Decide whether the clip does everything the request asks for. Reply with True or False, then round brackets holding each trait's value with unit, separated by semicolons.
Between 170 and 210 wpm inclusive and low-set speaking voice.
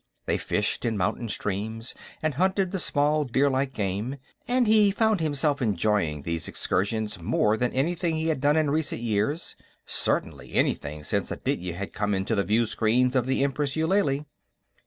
False (160 wpm; 130 Hz)